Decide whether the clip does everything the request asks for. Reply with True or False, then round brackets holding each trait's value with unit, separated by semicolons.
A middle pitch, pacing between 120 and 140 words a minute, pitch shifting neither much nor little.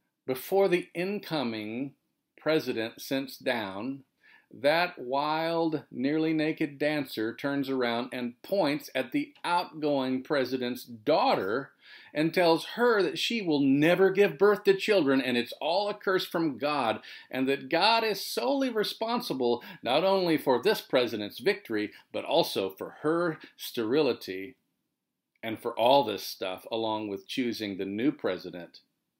False (150 Hz; 135 wpm; 6.8 semitones)